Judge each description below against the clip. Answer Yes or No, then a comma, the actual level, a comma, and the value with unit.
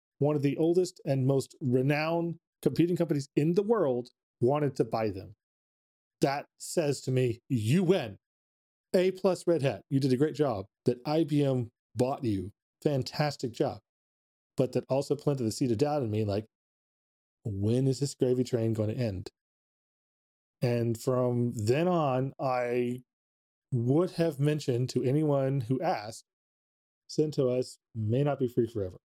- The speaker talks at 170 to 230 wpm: No, average, 155 wpm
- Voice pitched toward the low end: Yes, low, 130 Hz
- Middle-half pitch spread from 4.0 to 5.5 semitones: Yes, average, 4.6 semitones